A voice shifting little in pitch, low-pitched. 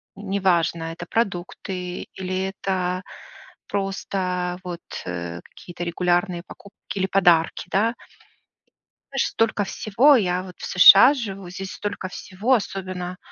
No: narrow, 2.0 semitones; medium, 185 Hz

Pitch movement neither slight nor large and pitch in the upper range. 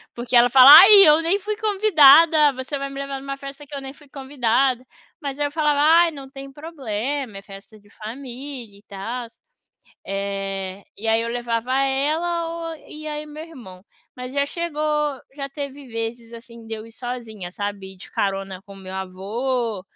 Yes: average, 4.7 semitones; very high, 265 Hz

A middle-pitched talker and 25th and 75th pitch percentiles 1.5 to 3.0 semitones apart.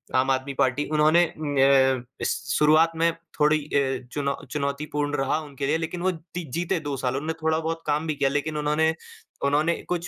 Yes: medium, 150 Hz; narrow, 2.4 semitones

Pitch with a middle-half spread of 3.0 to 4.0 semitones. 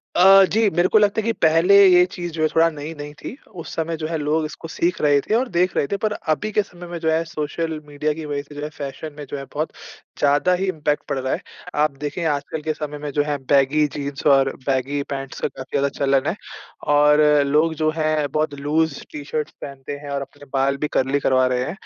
No: narrow, 2.5 semitones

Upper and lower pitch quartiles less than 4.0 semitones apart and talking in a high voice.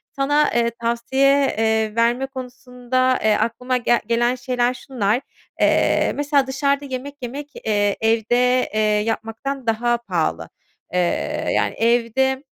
Yes: average, 2.9 semitones; high, 245 Hz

